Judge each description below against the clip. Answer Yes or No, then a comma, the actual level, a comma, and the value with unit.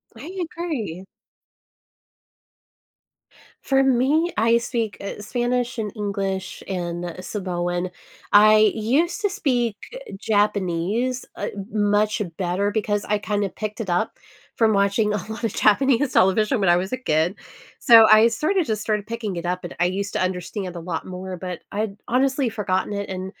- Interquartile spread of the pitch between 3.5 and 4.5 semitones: Yes, average, 3.8 semitones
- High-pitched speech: Yes, high, 210 Hz